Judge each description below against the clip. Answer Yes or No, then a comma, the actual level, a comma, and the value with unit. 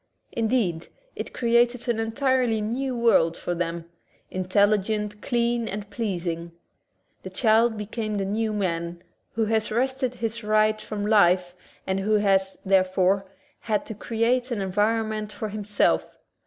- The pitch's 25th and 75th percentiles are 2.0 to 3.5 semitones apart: Yes, average, 3.0 semitones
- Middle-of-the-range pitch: No, high, 215 Hz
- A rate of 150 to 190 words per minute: No, average, 140 wpm